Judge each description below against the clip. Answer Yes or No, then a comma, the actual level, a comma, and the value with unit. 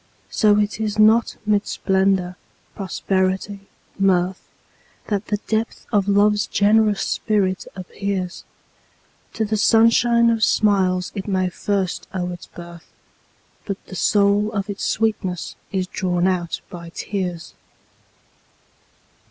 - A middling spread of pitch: No, narrow, 2.3 semitones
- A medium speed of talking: No, slow, 120 wpm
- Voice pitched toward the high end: Yes, high, 200 Hz